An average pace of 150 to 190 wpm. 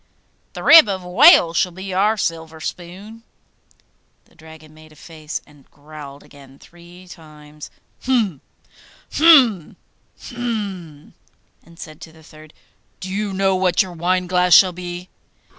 No: average, 140 wpm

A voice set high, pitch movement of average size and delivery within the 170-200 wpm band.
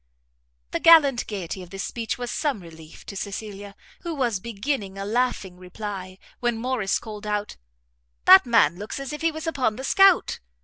Yes: high, 215 Hz; average, 5.0 semitones; average, 175 wpm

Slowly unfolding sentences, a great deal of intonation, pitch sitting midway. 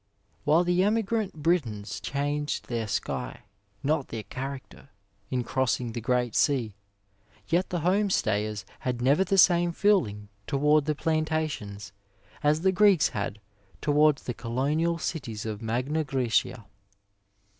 Yes: slow, 130 wpm; wide, 6.0 semitones; medium, 145 Hz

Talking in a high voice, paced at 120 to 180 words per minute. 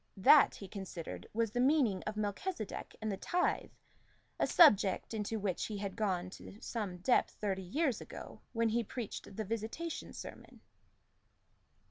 Yes: high, 215 Hz; average, 150 wpm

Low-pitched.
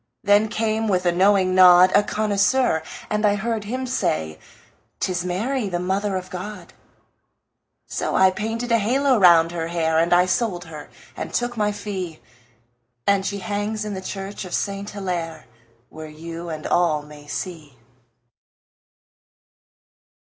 No: high, 190 Hz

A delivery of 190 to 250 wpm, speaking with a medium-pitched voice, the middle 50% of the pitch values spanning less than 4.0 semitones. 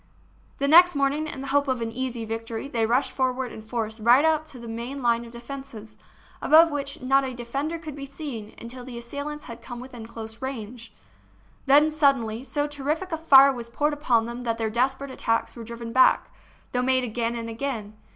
No: fast, 205 wpm; very high, 255 Hz; average, 3.3 semitones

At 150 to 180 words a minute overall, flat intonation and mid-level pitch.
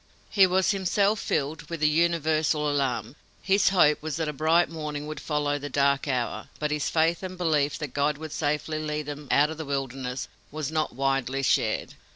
No: average, 195 wpm; narrow, 2.2 semitones; medium, 150 Hz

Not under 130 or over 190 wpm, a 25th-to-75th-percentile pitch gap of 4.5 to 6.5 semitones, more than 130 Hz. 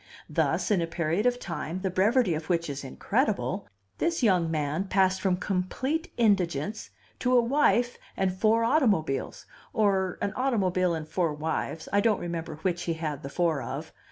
Yes: average, 170 wpm; average, 4.8 semitones; medium, 185 Hz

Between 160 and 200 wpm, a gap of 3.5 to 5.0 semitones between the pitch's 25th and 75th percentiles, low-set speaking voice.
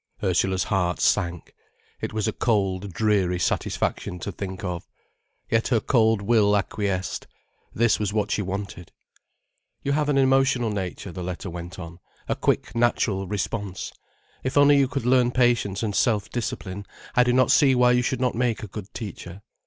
Yes: average, 170 wpm; average, 4.5 semitones; low, 105 Hz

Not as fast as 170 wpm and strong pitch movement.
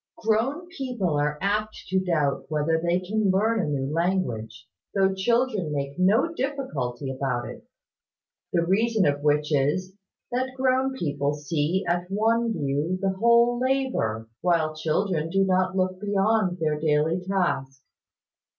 Yes: average, 140 wpm; wide, 6.5 semitones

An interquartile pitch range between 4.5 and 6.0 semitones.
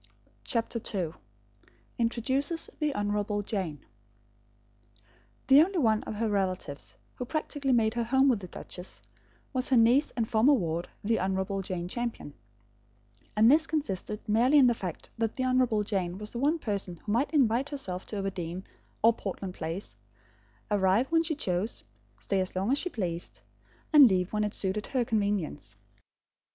Yes: average, 5.2 semitones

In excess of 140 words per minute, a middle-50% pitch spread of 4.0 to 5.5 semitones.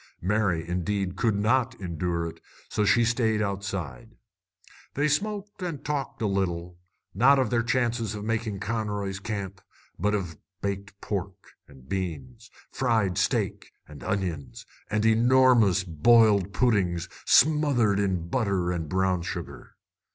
No: slow, 135 wpm; average, 4.3 semitones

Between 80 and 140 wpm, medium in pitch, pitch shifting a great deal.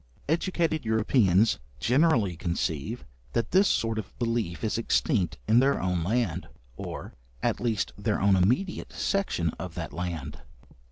No: slow, 135 wpm; low, 110 Hz; wide, 5.8 semitones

